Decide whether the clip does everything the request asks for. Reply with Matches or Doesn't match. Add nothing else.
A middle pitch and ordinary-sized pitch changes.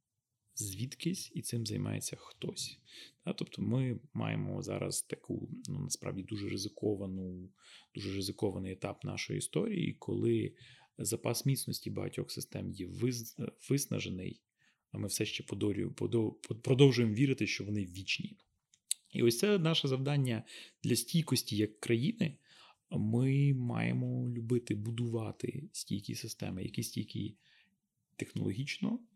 Doesn't match